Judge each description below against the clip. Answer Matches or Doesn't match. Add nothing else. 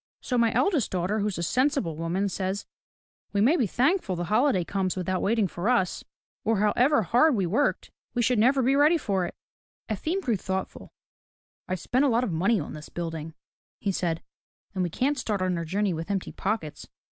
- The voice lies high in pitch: Matches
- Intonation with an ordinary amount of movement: Doesn't match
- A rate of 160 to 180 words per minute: Doesn't match